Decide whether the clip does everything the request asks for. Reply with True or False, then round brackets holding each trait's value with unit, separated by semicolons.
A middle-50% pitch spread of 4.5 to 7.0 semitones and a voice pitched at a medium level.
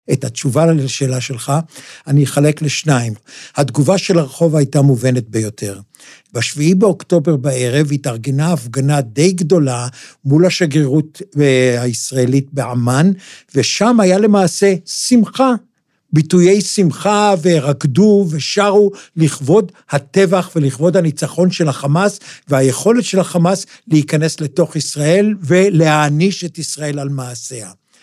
True (5.1 semitones; 155 Hz)